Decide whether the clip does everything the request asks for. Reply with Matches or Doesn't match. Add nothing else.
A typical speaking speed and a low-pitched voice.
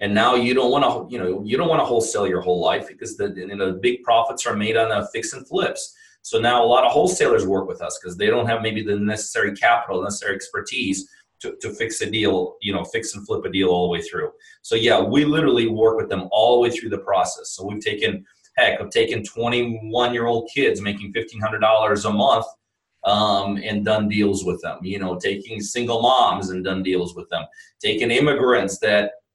Doesn't match